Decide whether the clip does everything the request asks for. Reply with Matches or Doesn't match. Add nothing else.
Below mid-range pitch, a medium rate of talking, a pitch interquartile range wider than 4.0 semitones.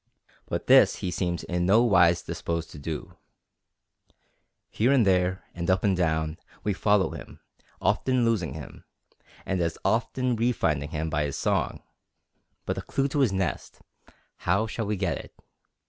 Matches